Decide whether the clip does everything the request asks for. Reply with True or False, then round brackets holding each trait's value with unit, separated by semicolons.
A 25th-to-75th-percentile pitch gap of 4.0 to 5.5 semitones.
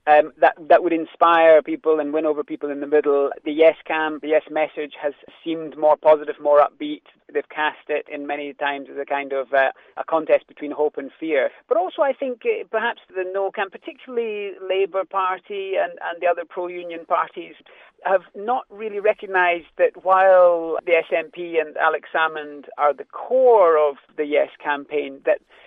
True (4.3 semitones)